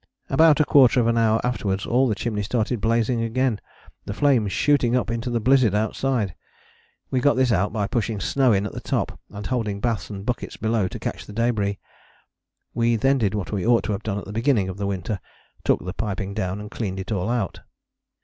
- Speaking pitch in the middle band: No, low, 110 Hz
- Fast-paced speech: Yes, fast, 215 wpm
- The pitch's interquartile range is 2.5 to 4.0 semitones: Yes, average, 3.4 semitones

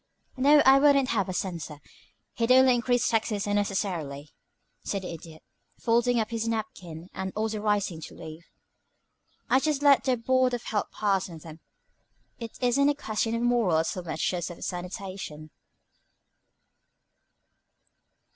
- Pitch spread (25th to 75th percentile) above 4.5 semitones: Yes, wide, 5.6 semitones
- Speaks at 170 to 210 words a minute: No, average, 145 wpm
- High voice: Yes, high, 210 Hz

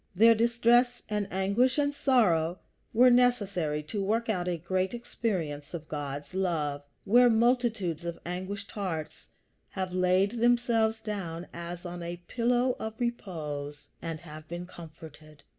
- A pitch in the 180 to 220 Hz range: Yes, high, 190 Hz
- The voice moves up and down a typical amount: No, wide, 5.8 semitones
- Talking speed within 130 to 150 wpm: Yes, average, 140 wpm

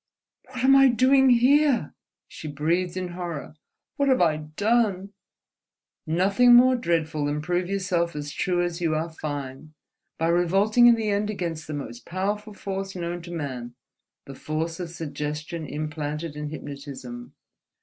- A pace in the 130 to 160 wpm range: Yes, average, 150 wpm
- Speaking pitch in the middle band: Yes, medium, 170 Hz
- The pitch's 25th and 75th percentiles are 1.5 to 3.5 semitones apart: No, average, 4.9 semitones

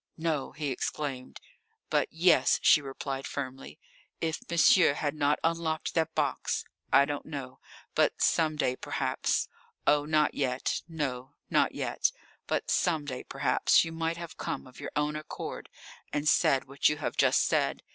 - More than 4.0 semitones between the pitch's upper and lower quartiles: No, average, 2.7 semitones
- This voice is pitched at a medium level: Yes, medium, 150 Hz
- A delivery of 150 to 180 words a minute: Yes, average, 155 wpm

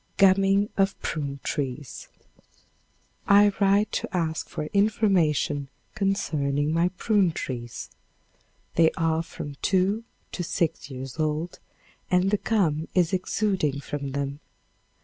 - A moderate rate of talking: No, slow, 115 wpm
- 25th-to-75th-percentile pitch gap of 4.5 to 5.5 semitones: Yes, average, 5.2 semitones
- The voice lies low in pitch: No, medium, 165 Hz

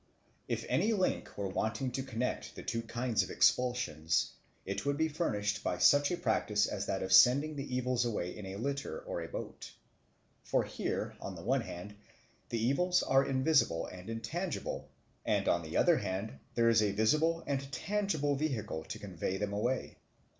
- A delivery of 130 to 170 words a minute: No, average, 180 wpm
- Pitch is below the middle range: Yes, low, 120 Hz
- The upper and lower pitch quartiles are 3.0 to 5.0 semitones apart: No, wide, 5.6 semitones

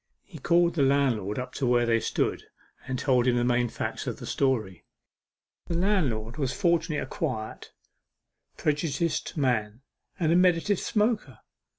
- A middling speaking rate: Yes, average, 155 wpm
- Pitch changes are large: Yes, wide, 5.8 semitones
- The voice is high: No, low, 135 Hz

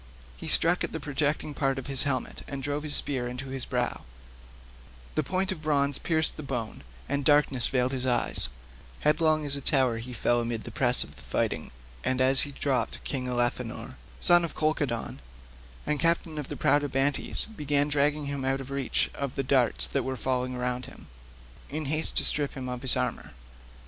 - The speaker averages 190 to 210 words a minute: Yes, average, 195 wpm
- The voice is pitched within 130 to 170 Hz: Yes, low, 135 Hz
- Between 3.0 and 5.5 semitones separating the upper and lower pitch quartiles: No, narrow, 2.6 semitones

